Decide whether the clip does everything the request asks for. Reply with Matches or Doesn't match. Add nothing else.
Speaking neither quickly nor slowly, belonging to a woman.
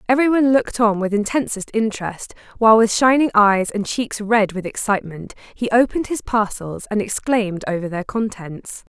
Matches